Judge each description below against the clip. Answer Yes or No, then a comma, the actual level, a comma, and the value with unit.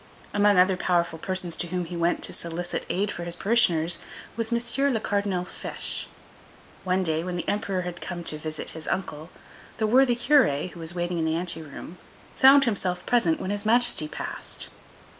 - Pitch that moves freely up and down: No, average, 3.8 semitones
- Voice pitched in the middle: Yes, medium, 180 Hz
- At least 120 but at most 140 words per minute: No, average, 180 wpm